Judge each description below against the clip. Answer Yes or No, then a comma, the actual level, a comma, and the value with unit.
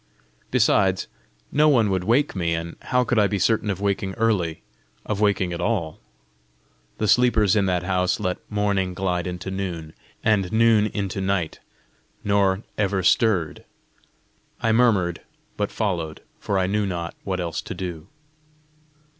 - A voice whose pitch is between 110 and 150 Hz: No, very low, 95 Hz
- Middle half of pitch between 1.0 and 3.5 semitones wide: Yes, average, 2.8 semitones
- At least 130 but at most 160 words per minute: Yes, average, 150 wpm